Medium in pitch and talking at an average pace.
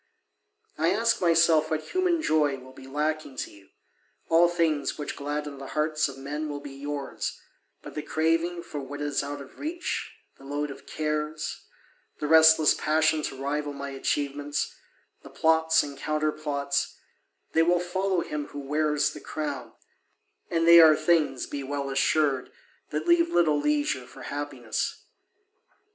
Yes: medium, 150 Hz; average, 155 wpm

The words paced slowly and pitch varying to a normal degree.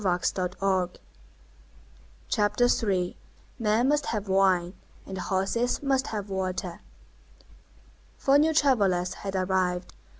Yes: slow, 90 wpm; average, 4.6 semitones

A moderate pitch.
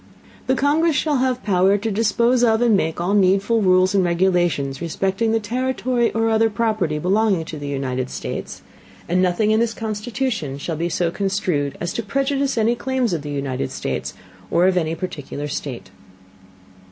No: high, 195 Hz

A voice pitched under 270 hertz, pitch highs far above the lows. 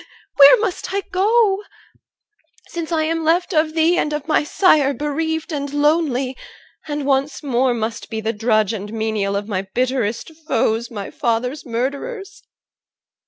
No: very high, 285 Hz; wide, 5.9 semitones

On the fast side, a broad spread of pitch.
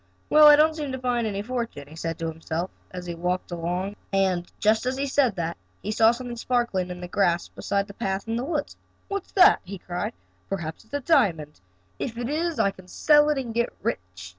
Yes: fast, 225 wpm; wide, 6.2 semitones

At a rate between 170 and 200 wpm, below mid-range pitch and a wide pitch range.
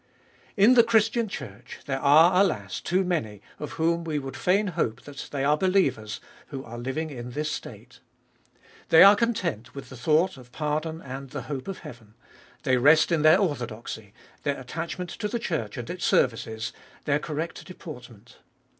No: average, 175 wpm; medium, 150 Hz; wide, 6.3 semitones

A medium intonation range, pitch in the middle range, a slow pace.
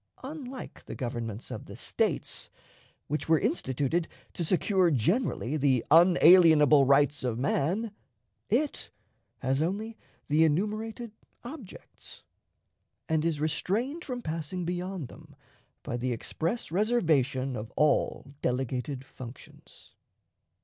No: wide, 7.0 semitones; medium, 160 Hz; slow, 110 wpm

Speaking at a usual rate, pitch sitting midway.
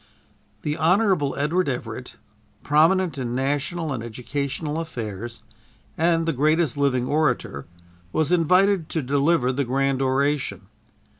No: slow, 120 wpm; medium, 145 Hz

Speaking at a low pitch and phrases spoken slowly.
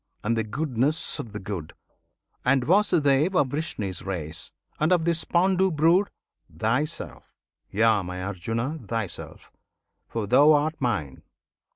Yes: low, 125 Hz; slow, 130 wpm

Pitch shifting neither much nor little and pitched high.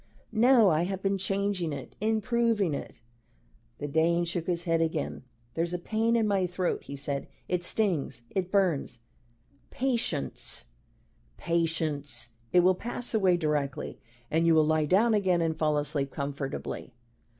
No: average, 4.5 semitones; medium, 175 Hz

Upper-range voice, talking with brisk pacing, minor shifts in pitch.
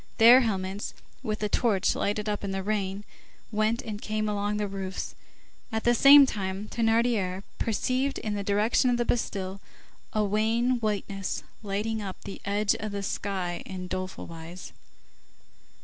No: high, 210 Hz; average, 155 wpm; narrow, 2.3 semitones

